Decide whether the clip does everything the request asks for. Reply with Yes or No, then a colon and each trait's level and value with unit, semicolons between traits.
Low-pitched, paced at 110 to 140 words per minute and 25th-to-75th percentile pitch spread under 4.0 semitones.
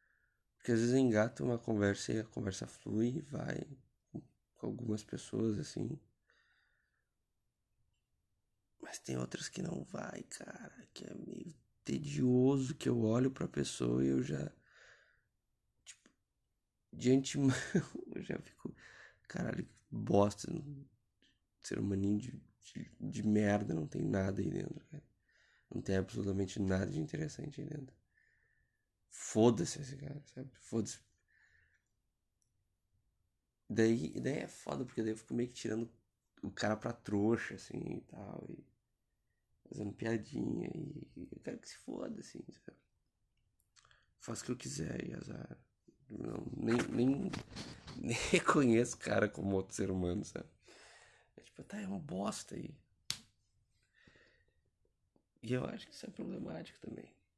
No: low, 115 Hz; average, 135 wpm; average, 4.4 semitones